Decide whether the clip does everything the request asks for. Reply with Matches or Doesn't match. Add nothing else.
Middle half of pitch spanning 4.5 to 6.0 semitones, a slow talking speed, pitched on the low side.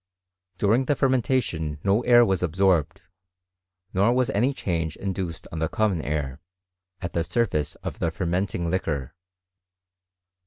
Matches